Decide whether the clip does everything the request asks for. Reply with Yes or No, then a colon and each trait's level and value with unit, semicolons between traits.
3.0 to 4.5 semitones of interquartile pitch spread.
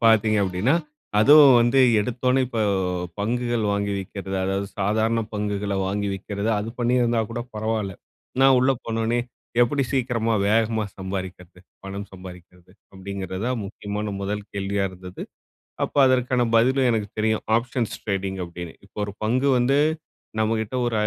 Yes: average, 3.4 semitones